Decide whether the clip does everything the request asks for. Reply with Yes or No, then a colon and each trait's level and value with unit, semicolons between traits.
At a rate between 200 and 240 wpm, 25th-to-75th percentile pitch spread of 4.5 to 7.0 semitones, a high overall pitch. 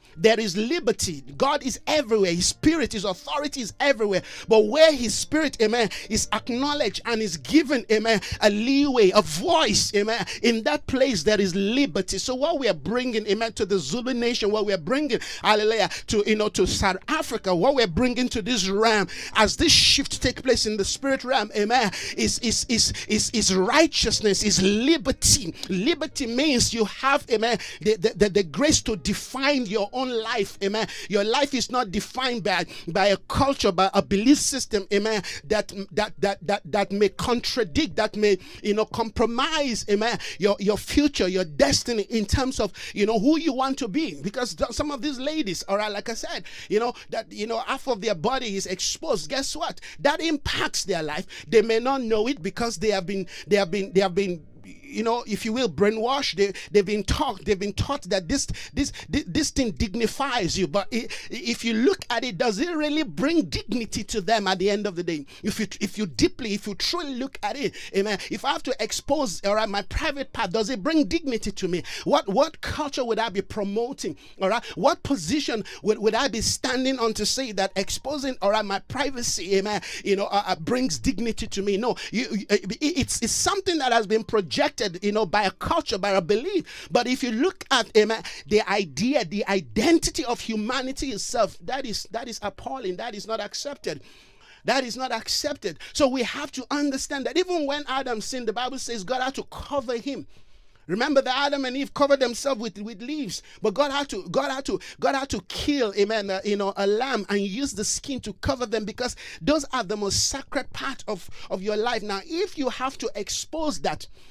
Yes: fast, 205 wpm; average, 4.8 semitones; high, 225 Hz